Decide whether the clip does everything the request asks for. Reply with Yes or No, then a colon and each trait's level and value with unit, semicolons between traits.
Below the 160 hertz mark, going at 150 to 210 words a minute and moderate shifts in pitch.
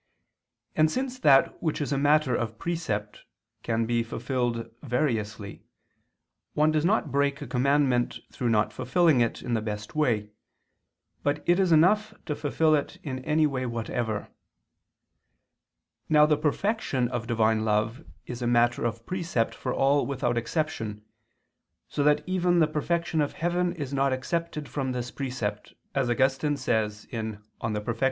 Yes: low, 135 Hz; average, 155 wpm; average, 4.8 semitones